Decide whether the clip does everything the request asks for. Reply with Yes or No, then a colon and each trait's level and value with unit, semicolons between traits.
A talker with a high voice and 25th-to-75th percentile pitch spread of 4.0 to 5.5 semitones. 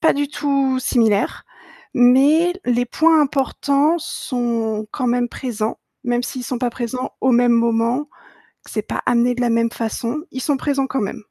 No: high, 245 Hz; average, 2.8 semitones